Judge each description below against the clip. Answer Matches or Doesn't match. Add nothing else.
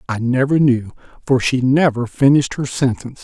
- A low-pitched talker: Matches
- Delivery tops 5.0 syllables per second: Matches